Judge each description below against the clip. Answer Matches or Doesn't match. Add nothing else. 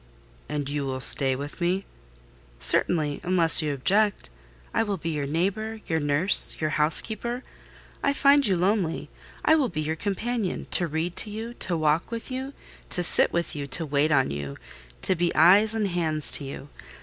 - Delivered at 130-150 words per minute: Doesn't match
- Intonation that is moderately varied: Doesn't match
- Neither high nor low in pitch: Matches